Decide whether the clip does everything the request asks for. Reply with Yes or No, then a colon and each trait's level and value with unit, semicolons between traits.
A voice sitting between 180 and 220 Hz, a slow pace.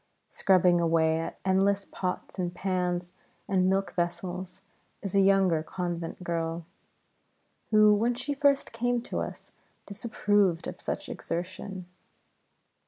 Yes: medium, 185 Hz; slow, 120 wpm